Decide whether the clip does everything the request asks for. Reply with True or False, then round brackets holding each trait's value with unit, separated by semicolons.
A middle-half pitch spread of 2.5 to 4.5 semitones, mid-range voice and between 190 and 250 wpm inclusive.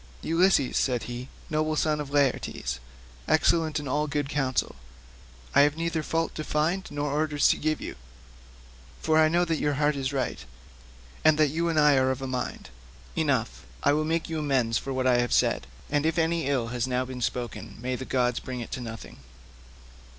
True (3.3 semitones; 145 Hz; 195 wpm)